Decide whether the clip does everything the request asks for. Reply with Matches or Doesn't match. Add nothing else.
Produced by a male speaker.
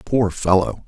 Matches